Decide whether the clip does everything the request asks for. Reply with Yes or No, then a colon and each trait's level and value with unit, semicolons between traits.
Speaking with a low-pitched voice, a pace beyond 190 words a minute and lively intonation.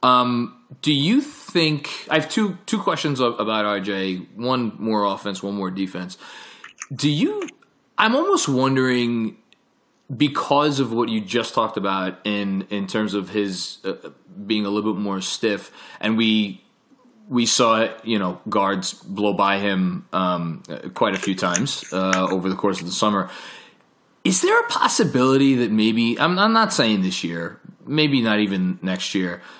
No: low, 110 Hz; average, 165 wpm; wide, 6.9 semitones